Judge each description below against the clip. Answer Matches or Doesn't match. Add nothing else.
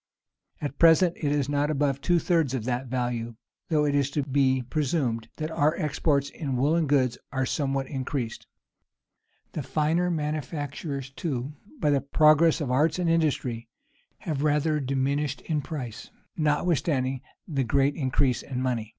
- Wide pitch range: Doesn't match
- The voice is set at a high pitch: Doesn't match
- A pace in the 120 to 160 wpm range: Matches